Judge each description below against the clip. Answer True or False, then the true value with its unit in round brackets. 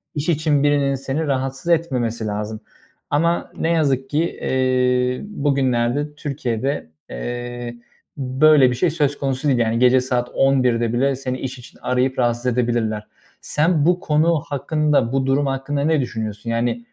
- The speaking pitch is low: True (130 Hz)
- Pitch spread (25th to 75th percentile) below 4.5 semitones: True (3.2 semitones)